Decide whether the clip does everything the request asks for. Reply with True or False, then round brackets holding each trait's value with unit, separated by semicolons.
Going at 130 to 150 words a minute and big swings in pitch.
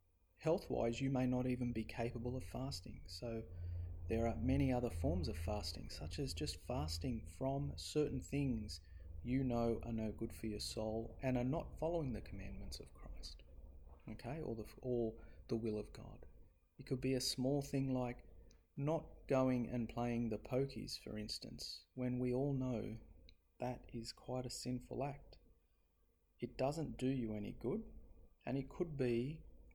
False (165 wpm; 6.7 semitones)